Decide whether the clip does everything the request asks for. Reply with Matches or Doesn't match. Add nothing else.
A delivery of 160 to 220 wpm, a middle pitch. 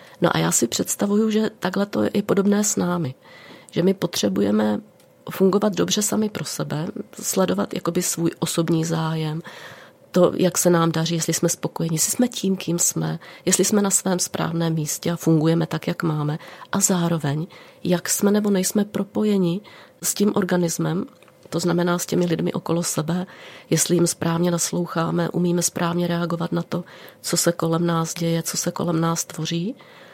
Matches